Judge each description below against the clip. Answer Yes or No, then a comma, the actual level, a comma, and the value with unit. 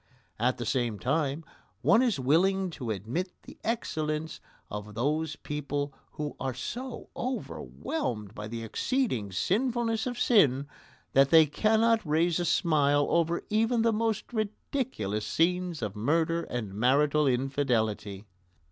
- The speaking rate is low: Yes, slow, 130 wpm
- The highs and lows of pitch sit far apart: Yes, wide, 8.6 semitones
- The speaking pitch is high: No, medium, 150 Hz